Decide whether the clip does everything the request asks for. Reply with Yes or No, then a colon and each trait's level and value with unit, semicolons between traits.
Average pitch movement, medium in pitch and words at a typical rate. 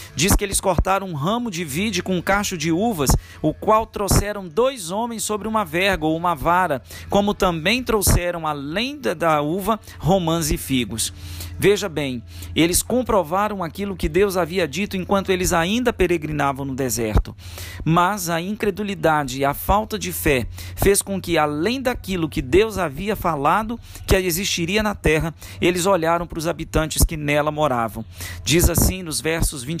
Yes: average, 4.8 semitones; medium, 175 Hz; average, 165 wpm